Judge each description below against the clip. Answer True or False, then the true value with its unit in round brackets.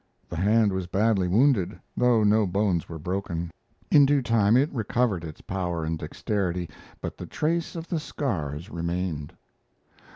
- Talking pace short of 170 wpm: True (155 wpm)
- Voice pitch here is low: True (100 Hz)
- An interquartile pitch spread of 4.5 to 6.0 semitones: True (5.1 semitones)